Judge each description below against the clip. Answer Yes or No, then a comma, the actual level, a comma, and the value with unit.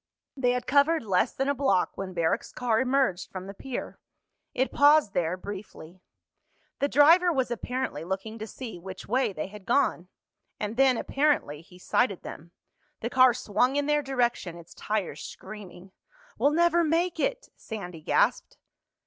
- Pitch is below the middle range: No, high, 235 Hz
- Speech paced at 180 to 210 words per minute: No, average, 160 wpm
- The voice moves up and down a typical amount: No, wide, 6.8 semitones